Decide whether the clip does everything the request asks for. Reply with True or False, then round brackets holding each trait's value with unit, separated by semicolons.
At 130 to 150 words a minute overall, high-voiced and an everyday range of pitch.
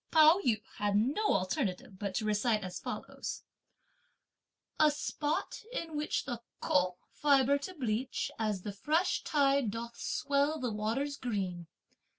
False (140 wpm; 245 Hz; 5.9 semitones)